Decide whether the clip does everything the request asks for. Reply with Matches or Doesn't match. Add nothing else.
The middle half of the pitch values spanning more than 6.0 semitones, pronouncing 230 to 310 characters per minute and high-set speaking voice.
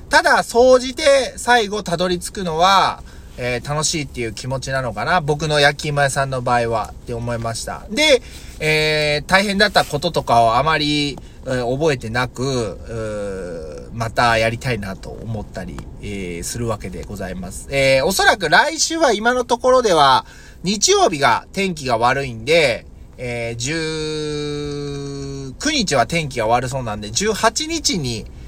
Doesn't match